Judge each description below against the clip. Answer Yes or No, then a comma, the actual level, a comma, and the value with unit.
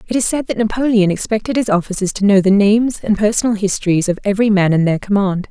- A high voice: Yes, high, 205 Hz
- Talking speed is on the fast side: Yes, fast, 230 wpm